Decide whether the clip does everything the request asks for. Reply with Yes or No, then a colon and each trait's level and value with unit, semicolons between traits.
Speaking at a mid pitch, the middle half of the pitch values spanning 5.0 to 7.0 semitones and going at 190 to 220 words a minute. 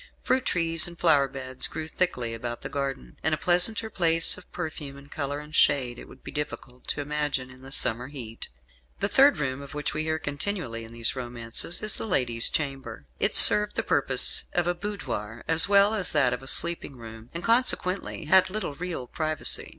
Yes: medium, 145 Hz; wide, 5.5 semitones; average, 200 wpm